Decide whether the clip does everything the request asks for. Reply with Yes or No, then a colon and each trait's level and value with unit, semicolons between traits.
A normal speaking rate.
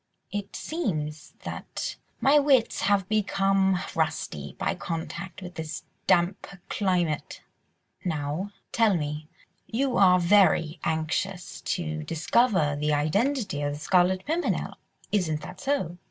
No: slow, 120 wpm